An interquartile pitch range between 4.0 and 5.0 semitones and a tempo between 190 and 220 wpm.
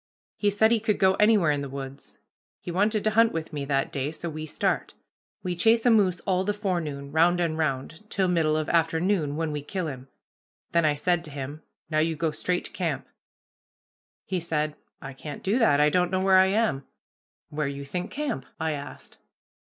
Yes: average, 4.4 semitones; fast, 205 wpm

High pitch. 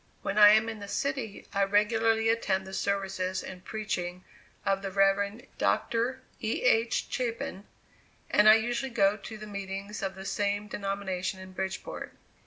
Yes: high, 200 Hz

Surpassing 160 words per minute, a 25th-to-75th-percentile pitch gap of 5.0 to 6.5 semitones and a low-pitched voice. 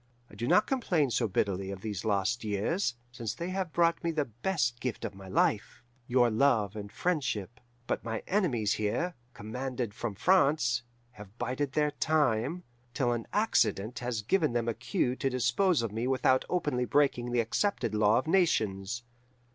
Yes: average, 170 wpm; wide, 5.4 semitones; low, 120 Hz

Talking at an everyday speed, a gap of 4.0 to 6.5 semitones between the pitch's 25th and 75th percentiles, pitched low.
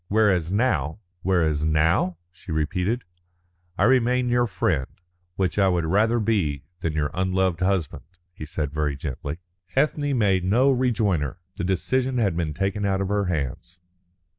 Yes: average, 155 wpm; wide, 5.6 semitones; very low, 95 Hz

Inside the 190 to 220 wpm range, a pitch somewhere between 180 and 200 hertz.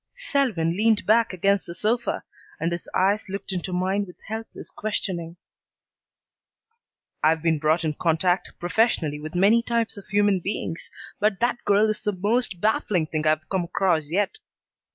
No: average, 155 wpm; high, 190 Hz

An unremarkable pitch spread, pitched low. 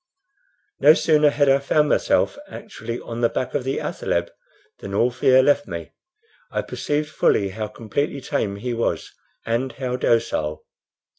Yes: average, 4.4 semitones; low, 125 Hz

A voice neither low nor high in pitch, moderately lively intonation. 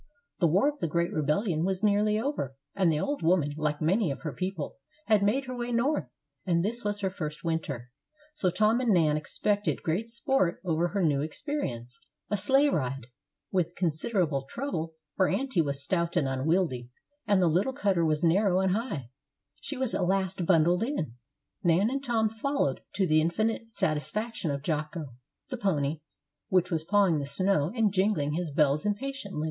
No: medium, 180 Hz; wide, 5.7 semitones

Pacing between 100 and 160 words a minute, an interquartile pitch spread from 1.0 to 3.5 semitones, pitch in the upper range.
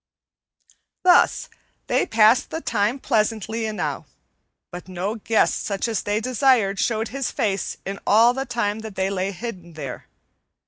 Yes: average, 145 wpm; average, 3.2 semitones; high, 215 Hz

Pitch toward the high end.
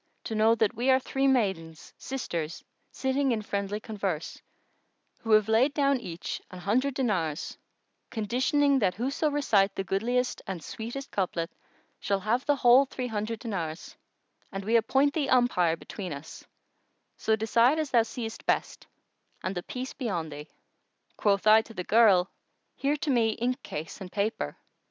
Yes: high, 220 Hz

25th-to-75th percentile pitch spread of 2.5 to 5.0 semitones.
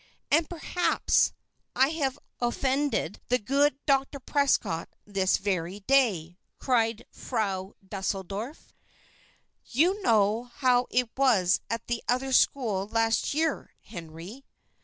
No: wide, 5.5 semitones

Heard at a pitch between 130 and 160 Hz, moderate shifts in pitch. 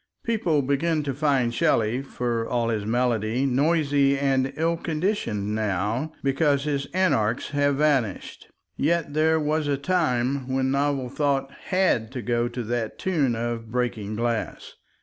Yes: low, 135 Hz; average, 4.0 semitones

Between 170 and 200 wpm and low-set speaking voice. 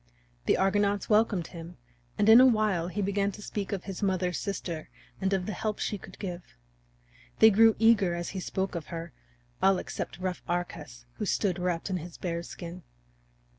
No: average, 185 wpm; high, 190 Hz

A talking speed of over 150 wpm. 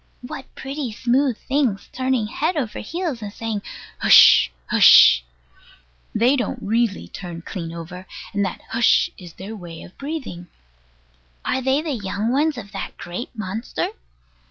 No: average, 145 wpm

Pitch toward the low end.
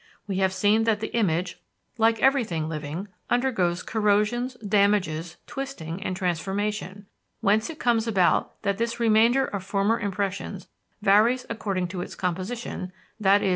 No: high, 205 Hz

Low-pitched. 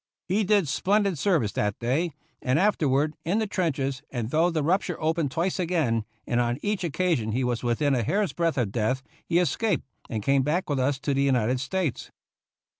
No: medium, 150 Hz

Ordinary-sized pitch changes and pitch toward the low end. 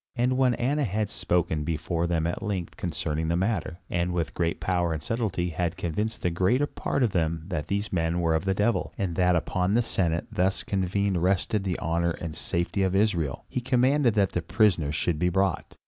Yes: average, 3.7 semitones; very low, 90 Hz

